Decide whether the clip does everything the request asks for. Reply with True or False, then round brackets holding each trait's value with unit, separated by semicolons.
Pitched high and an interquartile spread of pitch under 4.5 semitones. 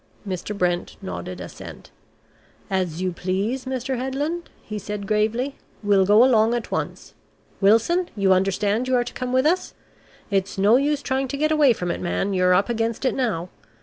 False (215 Hz; 5.3 semitones)